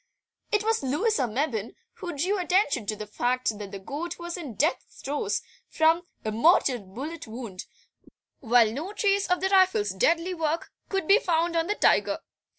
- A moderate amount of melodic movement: No, wide, 7.5 semitones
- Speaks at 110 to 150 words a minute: No, average, 170 wpm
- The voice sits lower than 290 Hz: No, very high, 315 Hz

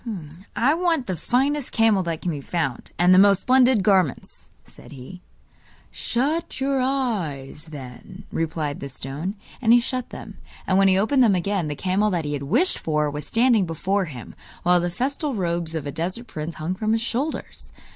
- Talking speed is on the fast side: No, average, 185 wpm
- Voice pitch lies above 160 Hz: Yes, medium, 185 Hz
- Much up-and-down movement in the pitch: Yes, wide, 7.3 semitones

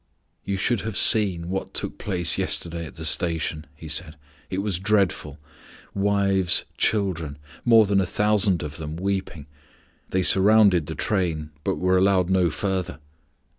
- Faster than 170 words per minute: No, average, 150 wpm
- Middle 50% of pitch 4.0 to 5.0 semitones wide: No, average, 3.3 semitones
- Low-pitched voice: Yes, very low, 95 Hz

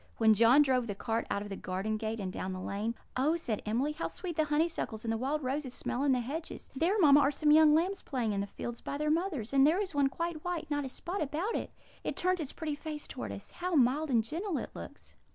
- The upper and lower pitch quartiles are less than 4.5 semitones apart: No, wide, 5.6 semitones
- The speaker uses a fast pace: Yes, fast, 260 wpm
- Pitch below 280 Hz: No, very high, 285 Hz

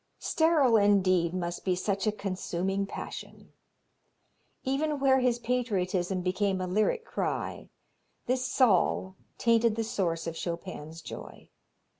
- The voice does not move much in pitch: No, average, 4.8 semitones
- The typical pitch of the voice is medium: No, high, 200 Hz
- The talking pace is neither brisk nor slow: No, slow, 120 wpm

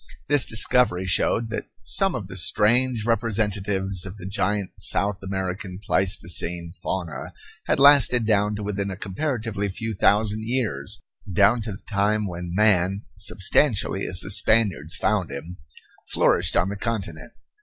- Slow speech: No, average, 145 wpm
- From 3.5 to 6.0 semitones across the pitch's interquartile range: No, average, 3.0 semitones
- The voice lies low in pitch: Yes, low, 100 Hz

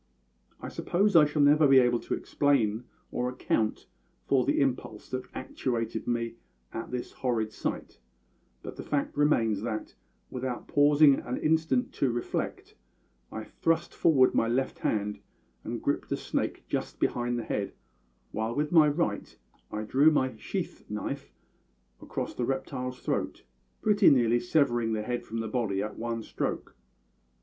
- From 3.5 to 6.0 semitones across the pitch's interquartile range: Yes, average, 4.0 semitones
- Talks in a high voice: No, low, 125 Hz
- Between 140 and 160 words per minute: Yes, average, 155 wpm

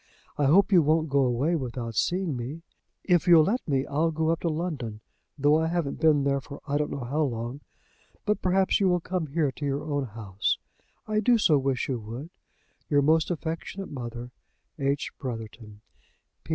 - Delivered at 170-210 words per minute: Yes, average, 185 wpm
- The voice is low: No, medium, 145 Hz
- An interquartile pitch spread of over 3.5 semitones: Yes, average, 4.2 semitones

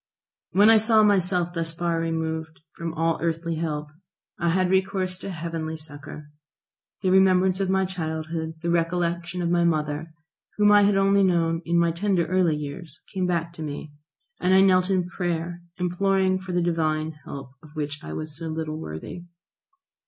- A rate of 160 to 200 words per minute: Yes, average, 175 wpm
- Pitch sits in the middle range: Yes, medium, 170 Hz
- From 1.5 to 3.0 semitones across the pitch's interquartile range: Yes, narrow, 2.6 semitones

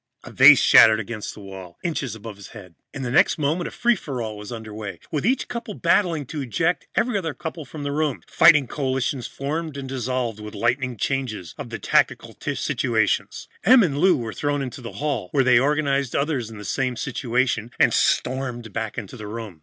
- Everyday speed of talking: No, fast, 210 wpm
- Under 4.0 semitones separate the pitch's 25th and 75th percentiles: No, average, 5.0 semitones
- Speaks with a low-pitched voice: Yes, low, 130 Hz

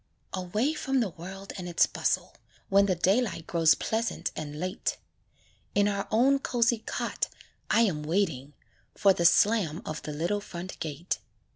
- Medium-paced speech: Yes, average, 155 wpm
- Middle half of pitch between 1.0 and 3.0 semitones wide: No, average, 4.6 semitones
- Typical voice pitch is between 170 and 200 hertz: Yes, high, 190 Hz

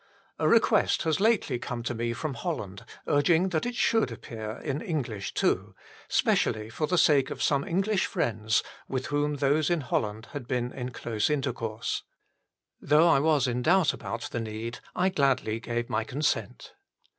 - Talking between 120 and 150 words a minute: No, average, 170 wpm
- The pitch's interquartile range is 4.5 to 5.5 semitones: Yes, average, 5.1 semitones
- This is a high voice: No, low, 135 Hz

